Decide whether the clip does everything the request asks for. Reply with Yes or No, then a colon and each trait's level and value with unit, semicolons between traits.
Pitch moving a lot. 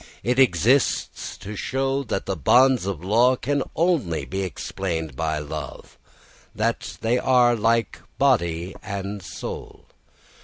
Yes: wide, 6.4 semitones